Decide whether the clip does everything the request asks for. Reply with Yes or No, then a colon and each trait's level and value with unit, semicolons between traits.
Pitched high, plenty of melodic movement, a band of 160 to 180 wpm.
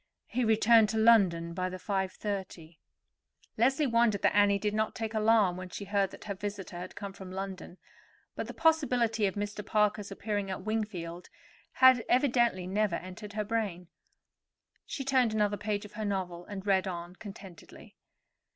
No: high, 205 Hz; average, 2.9 semitones; average, 165 wpm